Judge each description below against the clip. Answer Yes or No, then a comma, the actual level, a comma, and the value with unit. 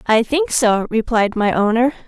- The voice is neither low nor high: No, high, 235 Hz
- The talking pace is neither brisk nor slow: Yes, average, 175 wpm